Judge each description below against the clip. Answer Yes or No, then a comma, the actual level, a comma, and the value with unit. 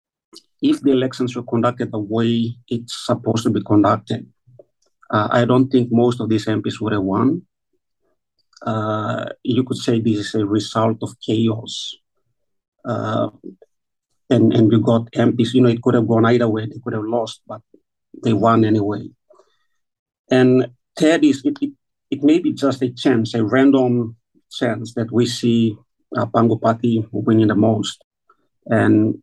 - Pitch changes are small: Yes, narrow, 2.3 semitones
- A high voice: No, low, 115 Hz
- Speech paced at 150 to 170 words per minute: Yes, average, 160 wpm